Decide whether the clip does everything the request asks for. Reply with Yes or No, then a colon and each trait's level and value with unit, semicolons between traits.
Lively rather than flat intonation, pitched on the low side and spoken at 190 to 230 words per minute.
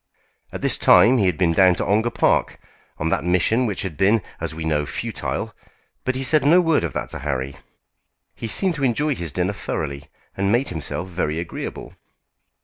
Yes: wide, 7.2 semitones; very low, 95 Hz; average, 195 wpm